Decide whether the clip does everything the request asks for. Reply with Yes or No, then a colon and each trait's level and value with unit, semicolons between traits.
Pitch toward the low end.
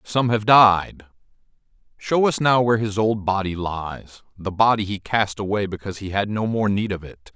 Yes: low, 105 Hz